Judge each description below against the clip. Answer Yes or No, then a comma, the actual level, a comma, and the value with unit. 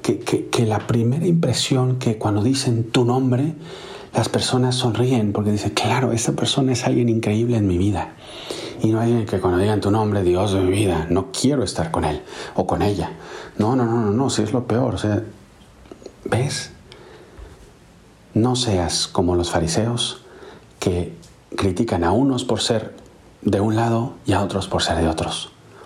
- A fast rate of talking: No, average, 180 wpm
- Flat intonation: No, average, 4.0 semitones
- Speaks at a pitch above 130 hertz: No, low, 110 Hz